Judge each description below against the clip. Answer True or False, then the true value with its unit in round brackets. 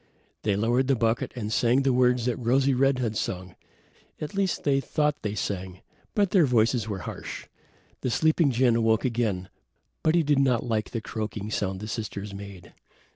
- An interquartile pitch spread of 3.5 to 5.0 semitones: True (4.3 semitones)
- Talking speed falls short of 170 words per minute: False (185 wpm)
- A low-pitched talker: True (120 Hz)